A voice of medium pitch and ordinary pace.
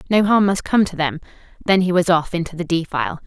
No: medium, 180 Hz; fast, 240 wpm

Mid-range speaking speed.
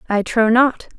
Yes: average, 180 wpm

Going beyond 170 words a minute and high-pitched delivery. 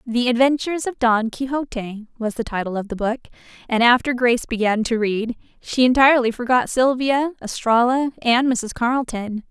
No: average, 160 wpm; high, 240 Hz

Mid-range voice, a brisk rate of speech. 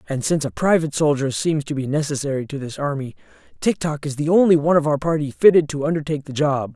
Yes: medium, 145 Hz; fast, 230 wpm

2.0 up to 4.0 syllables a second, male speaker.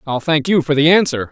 No: 6.0 syllables/s; male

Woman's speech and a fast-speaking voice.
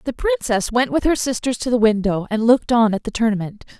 Yes: female; fast, 235 wpm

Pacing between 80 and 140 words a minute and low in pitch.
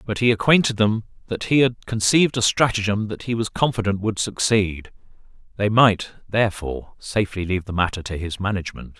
No: average, 175 wpm; low, 105 Hz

